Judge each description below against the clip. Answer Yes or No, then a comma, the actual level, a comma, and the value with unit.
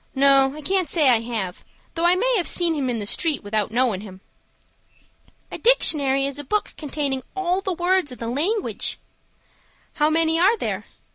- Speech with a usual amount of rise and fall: No, wide, 5.8 semitones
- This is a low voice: No, very high, 295 Hz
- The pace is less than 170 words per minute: No, average, 185 wpm